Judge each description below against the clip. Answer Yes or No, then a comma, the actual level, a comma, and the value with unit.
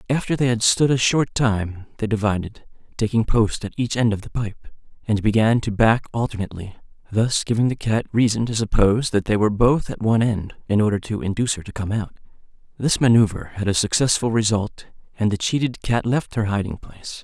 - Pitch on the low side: Yes, low, 110 Hz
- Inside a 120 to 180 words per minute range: No, average, 200 wpm